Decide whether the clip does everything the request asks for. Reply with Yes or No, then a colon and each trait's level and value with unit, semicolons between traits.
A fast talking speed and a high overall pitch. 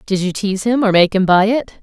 Yes: fast, 295 wpm; high, 205 Hz